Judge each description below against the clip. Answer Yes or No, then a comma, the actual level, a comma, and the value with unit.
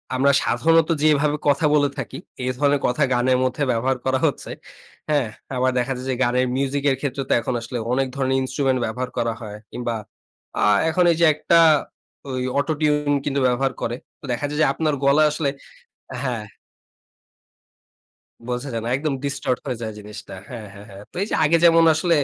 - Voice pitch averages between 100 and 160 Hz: Yes, low, 135 Hz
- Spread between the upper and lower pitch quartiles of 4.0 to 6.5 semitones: No, average, 3.1 semitones